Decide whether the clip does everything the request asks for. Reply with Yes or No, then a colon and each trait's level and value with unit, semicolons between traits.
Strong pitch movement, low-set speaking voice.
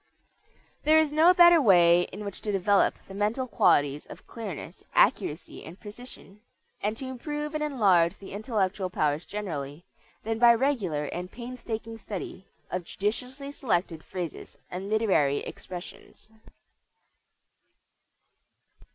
No: wide, 5.8 semitones; high, 205 Hz